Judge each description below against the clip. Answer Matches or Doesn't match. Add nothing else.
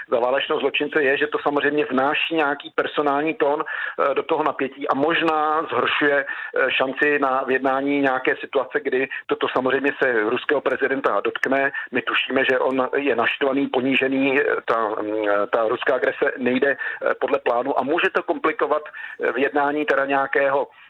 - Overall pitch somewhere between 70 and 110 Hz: Doesn't match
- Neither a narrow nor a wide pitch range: Doesn't match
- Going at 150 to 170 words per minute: Doesn't match